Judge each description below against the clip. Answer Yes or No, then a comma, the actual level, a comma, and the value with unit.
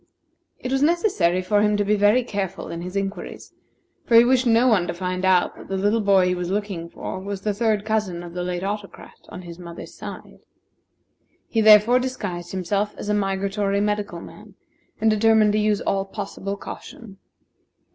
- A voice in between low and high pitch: No, high, 205 Hz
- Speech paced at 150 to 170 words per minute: No, average, 185 wpm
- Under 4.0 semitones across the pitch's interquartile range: Yes, narrow, 2.4 semitones